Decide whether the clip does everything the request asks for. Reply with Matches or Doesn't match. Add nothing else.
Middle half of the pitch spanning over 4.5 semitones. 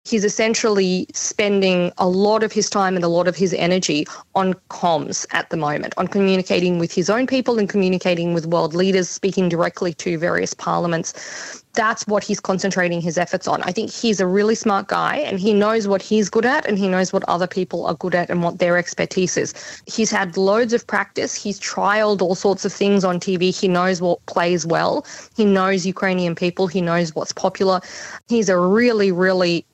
Doesn't match